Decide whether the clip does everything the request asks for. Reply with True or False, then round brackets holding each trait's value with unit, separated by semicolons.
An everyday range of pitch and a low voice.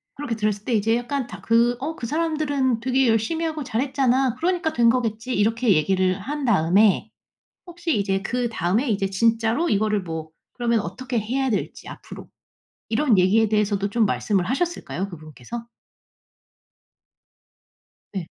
False (4.6 semitones; 230 Hz)